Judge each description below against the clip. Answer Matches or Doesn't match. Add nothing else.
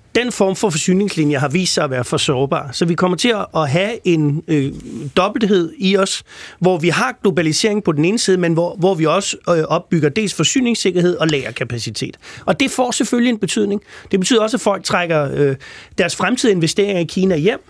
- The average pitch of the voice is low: Doesn't match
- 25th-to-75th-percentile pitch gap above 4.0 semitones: Matches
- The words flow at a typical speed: Matches